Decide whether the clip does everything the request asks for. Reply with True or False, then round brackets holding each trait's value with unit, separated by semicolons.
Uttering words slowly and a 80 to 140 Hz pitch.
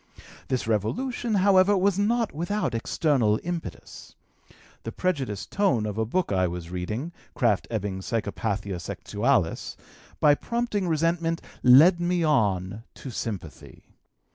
True (120 wpm; 135 Hz)